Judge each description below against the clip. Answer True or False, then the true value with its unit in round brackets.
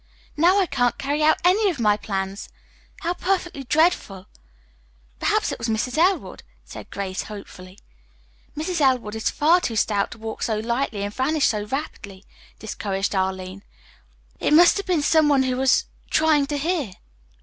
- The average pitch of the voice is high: True (260 Hz)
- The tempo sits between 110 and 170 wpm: True (165 wpm)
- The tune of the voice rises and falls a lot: True (7.3 semitones)